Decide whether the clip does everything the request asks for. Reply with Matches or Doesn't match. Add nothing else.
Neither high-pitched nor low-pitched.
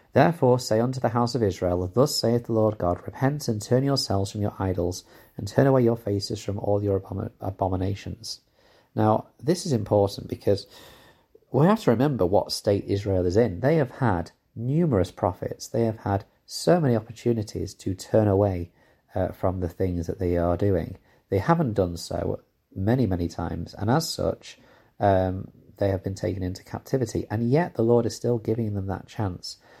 Doesn't match